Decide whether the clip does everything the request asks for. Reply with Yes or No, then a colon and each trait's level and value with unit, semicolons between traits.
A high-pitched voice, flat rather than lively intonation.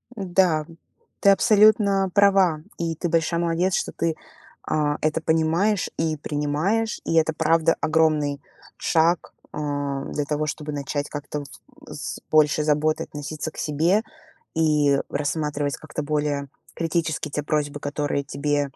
No: medium, 155 Hz; narrow, 2.2 semitones